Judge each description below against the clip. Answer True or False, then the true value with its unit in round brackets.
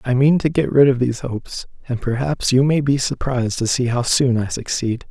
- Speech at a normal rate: False (235 wpm)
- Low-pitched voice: True (130 Hz)